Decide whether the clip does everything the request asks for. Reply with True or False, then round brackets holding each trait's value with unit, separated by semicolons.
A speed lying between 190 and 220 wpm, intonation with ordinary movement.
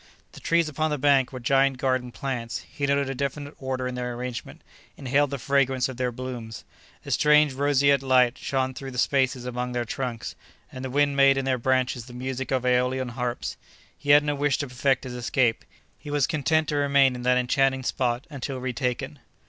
False (195 wpm; 2.0 semitones)